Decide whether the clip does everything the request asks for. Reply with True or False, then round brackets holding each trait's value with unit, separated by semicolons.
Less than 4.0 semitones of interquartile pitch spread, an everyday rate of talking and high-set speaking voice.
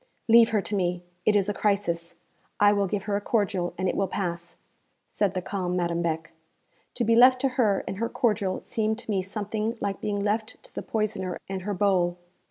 False (2.8 semitones; 210 wpm; 200 Hz)